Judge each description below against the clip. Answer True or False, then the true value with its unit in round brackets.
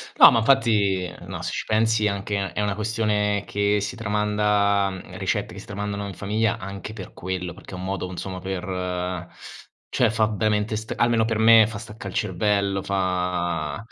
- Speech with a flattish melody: True (2.3 semitones)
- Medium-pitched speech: False (100 Hz)